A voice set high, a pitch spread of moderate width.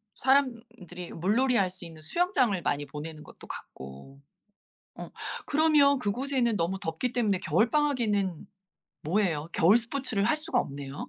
No: high, 205 Hz; wide, 7.9 semitones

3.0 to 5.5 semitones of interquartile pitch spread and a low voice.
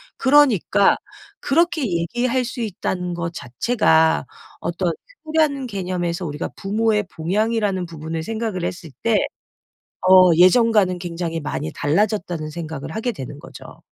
No: average, 5.2 semitones; medium, 185 Hz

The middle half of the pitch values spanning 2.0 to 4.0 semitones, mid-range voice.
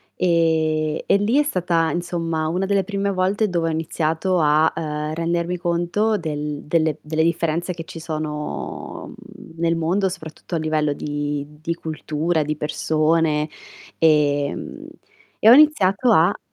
Yes: narrow, 2.5 semitones; medium, 165 Hz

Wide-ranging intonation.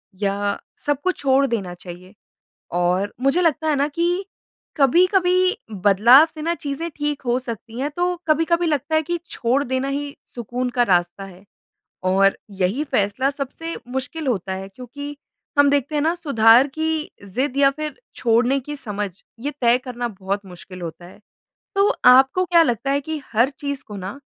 Yes: wide, 6.5 semitones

